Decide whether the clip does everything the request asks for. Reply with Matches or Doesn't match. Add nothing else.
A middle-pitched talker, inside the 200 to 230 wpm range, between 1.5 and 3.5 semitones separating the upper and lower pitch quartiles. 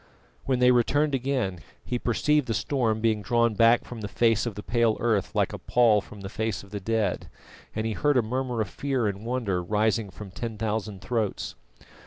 Doesn't match